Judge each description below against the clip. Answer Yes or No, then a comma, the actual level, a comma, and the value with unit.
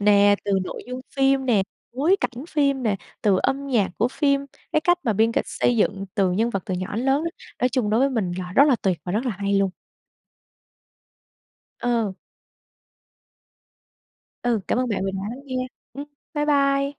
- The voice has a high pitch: Yes, high, 240 Hz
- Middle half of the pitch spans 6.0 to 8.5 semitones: No, average, 5.2 semitones